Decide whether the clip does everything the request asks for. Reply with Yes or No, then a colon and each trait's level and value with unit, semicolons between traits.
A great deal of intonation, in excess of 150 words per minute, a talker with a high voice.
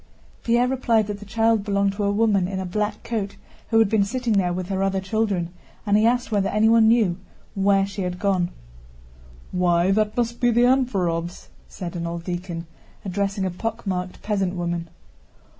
No: average, 3.5 semitones; average, 180 wpm; high, 200 Hz